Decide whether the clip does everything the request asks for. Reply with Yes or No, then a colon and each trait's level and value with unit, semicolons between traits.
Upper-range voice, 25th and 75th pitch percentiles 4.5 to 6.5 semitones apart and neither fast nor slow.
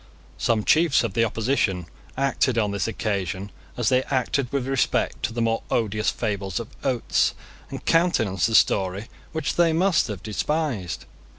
No: low, 115 Hz; average, 5.1 semitones; average, 160 wpm